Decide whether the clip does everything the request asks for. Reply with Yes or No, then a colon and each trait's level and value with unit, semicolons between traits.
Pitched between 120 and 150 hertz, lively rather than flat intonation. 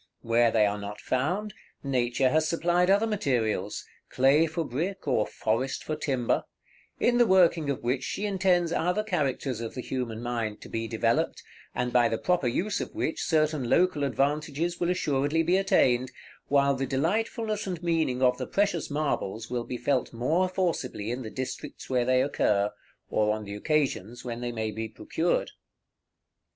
Yes: low, 135 Hz; wide, 6.1 semitones